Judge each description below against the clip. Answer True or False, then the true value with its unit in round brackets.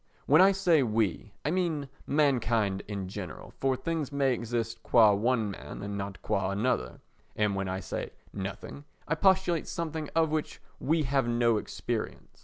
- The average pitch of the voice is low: True (125 Hz)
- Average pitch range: False (7.0 semitones)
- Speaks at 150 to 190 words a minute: True (160 wpm)